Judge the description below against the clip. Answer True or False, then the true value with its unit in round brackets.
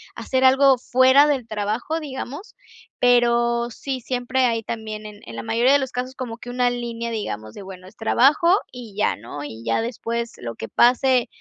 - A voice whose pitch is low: False (240 Hz)